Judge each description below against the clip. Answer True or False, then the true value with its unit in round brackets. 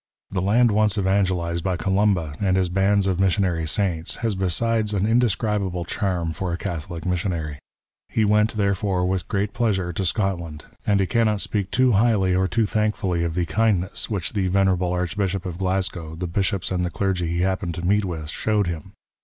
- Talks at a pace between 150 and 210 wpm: True (185 wpm)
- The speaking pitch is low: True (95 Hz)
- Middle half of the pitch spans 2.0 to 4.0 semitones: True (2.7 semitones)